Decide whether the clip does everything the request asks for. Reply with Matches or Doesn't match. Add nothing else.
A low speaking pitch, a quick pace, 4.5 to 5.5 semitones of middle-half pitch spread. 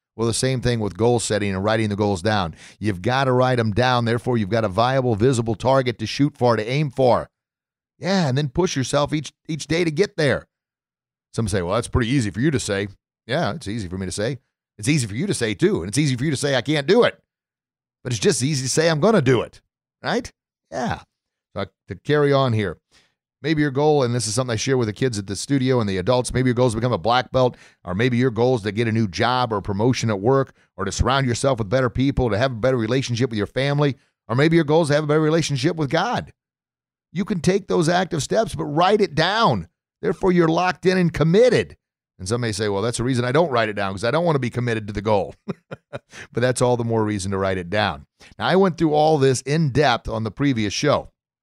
Matches